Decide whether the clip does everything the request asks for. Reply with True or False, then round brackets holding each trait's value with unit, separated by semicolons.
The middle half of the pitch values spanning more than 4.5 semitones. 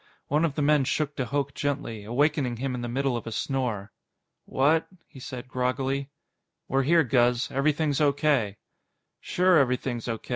False (2.9 semitones)